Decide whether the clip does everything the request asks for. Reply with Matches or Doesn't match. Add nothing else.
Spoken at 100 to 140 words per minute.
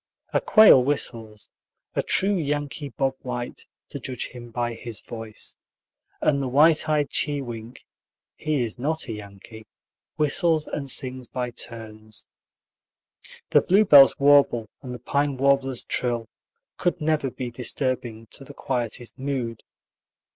Matches